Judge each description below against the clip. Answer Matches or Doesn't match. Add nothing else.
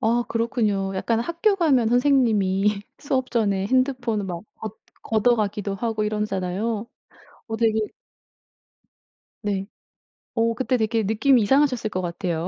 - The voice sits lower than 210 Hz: Doesn't match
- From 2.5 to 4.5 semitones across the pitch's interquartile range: Matches